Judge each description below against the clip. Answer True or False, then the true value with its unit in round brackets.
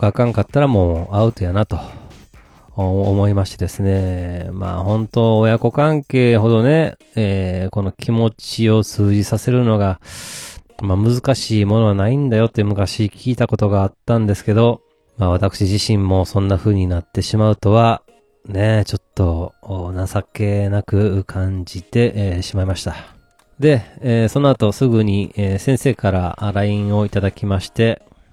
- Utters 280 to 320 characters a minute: True (300 characters per minute)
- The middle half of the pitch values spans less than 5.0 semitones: True (2.9 semitones)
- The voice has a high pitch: False (105 Hz)